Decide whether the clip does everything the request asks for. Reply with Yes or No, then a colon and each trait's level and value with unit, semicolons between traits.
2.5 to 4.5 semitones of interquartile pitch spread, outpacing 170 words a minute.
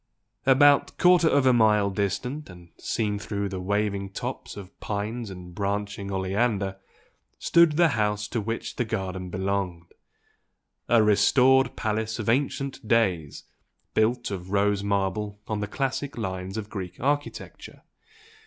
No: average, 3.7 semitones; slow, 135 wpm